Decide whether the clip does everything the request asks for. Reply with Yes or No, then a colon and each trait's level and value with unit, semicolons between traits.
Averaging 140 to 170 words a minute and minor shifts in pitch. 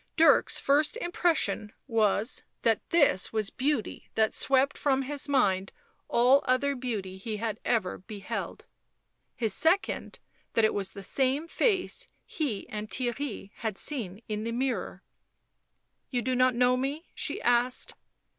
No: average, 145 wpm; average, 4.5 semitones